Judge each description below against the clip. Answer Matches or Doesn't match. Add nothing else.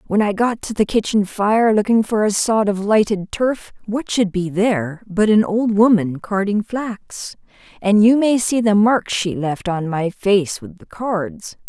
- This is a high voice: Matches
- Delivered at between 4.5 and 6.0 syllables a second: Doesn't match